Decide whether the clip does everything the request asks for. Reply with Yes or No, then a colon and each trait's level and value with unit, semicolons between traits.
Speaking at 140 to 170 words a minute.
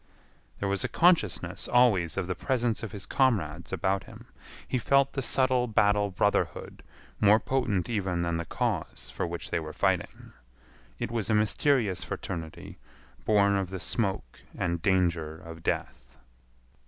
Yes: average, 155 wpm